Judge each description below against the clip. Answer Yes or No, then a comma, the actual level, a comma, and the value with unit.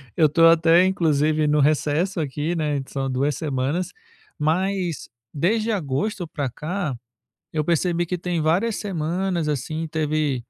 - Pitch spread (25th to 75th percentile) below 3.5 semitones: Yes, average, 3.1 semitones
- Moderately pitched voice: Yes, medium, 160 Hz